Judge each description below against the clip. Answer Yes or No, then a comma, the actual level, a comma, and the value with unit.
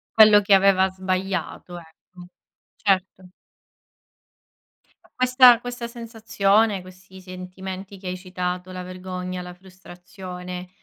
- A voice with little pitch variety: Yes, narrow, 1.6 semitones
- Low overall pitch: No, medium, 185 Hz